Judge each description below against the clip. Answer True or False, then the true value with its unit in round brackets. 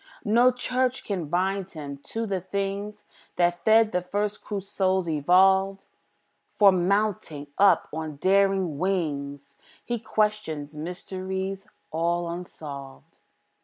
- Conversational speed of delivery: False (115 wpm)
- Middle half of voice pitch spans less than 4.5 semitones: True (3.4 semitones)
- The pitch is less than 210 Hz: True (190 Hz)